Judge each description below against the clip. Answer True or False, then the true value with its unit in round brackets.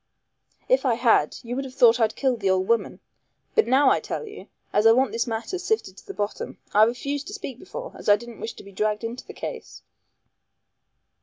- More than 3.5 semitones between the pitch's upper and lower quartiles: True (4.0 semitones)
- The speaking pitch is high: True (235 Hz)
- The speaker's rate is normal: False (220 wpm)